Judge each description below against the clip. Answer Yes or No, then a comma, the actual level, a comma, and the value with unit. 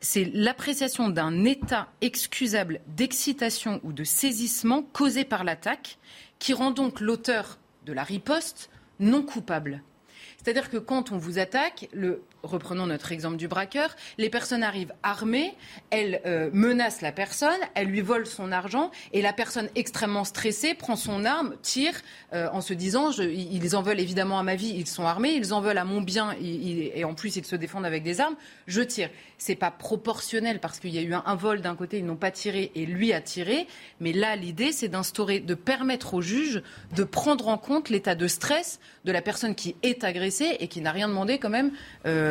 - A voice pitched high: Yes, high, 210 Hz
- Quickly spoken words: No, average, 200 wpm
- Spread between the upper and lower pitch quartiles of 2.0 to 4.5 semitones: No, average, 5.3 semitones